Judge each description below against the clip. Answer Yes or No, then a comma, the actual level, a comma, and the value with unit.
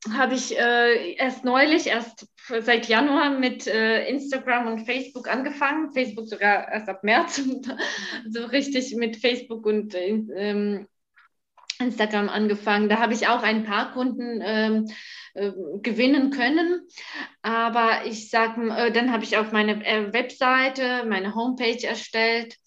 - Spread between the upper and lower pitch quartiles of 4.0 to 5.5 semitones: No, average, 2.9 semitones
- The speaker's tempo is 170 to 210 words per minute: No, average, 135 wpm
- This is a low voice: No, high, 230 Hz